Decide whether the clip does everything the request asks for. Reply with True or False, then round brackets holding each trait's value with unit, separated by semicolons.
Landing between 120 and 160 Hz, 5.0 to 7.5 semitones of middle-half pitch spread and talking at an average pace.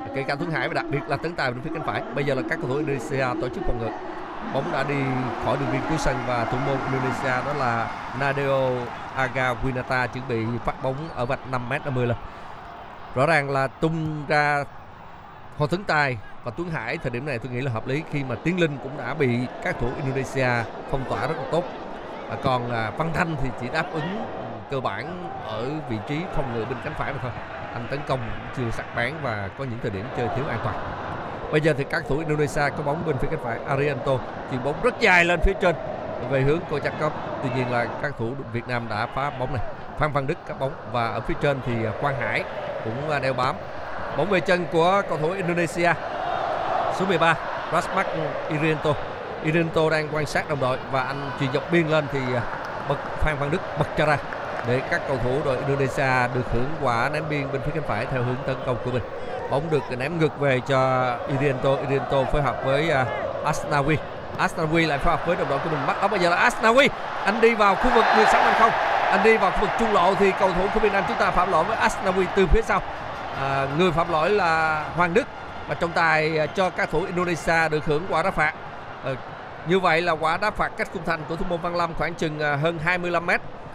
False (140 Hz; 4.4 semitones; 235 wpm)